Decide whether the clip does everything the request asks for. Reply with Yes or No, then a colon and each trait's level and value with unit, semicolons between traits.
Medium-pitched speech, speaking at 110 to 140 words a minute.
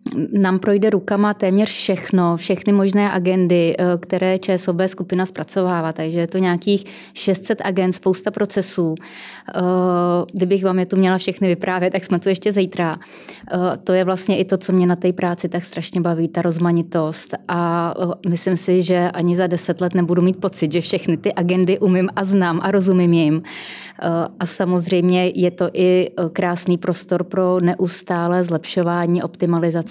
No: medium, 180 Hz; average, 160 wpm